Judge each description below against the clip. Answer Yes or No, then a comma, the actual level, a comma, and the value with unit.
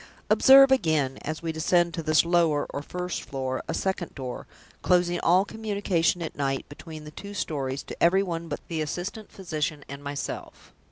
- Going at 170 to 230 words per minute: Yes, average, 175 wpm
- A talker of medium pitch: Yes, medium, 165 Hz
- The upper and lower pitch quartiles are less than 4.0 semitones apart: Yes, average, 3.6 semitones